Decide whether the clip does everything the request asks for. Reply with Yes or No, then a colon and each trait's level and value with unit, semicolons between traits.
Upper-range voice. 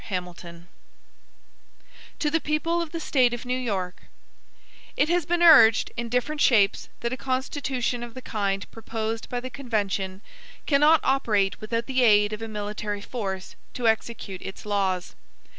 Yes: high, 230 Hz